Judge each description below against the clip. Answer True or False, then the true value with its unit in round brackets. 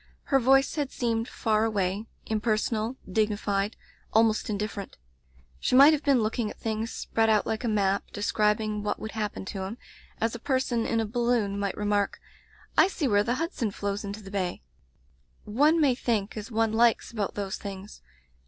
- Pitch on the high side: True (220 Hz)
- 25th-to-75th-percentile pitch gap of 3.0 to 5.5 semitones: False (2.6 semitones)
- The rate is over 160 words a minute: True (180 wpm)